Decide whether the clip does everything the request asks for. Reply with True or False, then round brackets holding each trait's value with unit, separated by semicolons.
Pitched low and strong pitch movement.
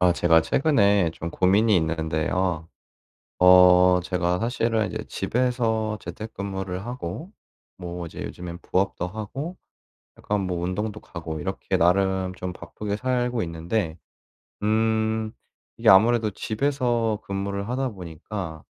False (100 Hz; 3.8 semitones)